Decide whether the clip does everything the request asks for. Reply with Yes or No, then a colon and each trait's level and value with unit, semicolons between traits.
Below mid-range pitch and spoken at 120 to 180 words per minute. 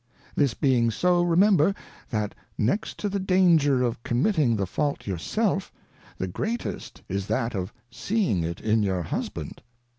Yes: low, 130 Hz; average, 150 wpm